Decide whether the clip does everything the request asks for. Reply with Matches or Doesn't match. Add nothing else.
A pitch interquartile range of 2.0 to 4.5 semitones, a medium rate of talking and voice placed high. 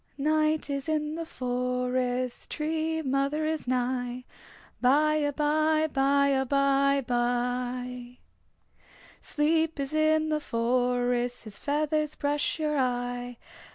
Doesn't match